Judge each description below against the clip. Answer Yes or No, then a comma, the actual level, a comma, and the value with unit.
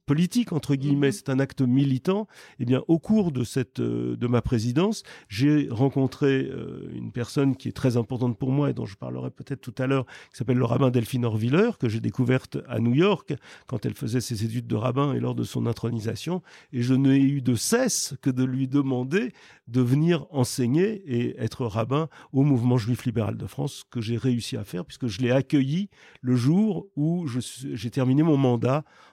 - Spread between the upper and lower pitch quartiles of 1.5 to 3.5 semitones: Yes, average, 2.9 semitones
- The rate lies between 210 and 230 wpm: No, average, 200 wpm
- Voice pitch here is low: Yes, low, 130 Hz